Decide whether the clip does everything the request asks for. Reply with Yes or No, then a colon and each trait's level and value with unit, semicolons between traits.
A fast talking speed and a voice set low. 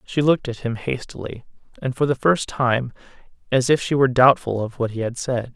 Yes: fast, 215 wpm; low, 125 Hz